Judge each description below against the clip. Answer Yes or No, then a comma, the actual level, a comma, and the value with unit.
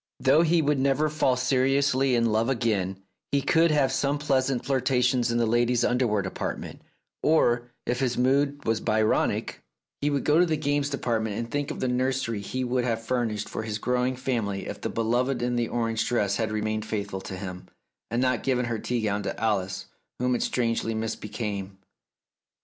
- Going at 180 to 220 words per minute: Yes, average, 185 wpm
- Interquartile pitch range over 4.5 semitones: No, average, 3.4 semitones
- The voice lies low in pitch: Yes, low, 120 Hz